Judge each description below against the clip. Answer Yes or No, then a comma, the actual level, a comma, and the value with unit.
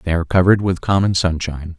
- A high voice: No, very low, 90 Hz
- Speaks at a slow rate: No, average, 200 wpm